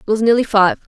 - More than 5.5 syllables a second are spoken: Yes, 5.9 syllables/s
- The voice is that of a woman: Yes, female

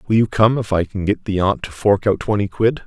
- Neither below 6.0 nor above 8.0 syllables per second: No, 5.6 syllables/s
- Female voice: No, male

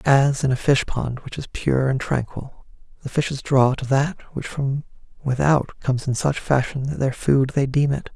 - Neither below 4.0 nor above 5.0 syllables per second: Yes, 4.7 syllables/s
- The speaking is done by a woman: No, male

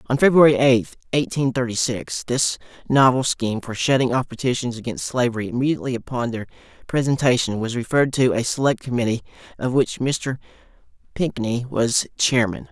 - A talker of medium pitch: No, low, 125 Hz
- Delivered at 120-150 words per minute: Yes, average, 145 wpm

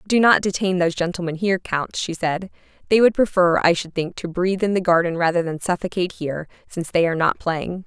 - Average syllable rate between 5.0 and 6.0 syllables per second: No, 6.2 syllables/s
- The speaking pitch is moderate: Yes, medium, 180 Hz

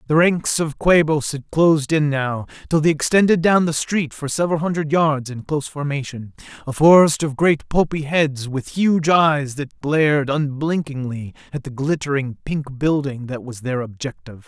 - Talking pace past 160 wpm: Yes, average, 170 wpm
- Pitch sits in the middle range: Yes, medium, 145 Hz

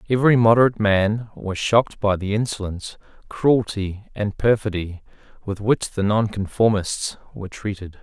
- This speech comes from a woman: No, male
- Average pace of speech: No, slow, 125 wpm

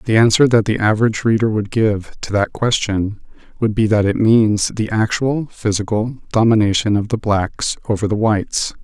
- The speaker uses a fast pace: No, average, 175 wpm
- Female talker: No, male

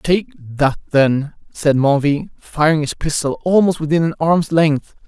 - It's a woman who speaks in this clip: No, male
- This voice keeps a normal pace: Yes, average, 155 wpm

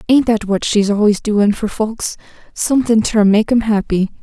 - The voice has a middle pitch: No, high, 215 Hz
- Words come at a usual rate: Yes, average, 170 wpm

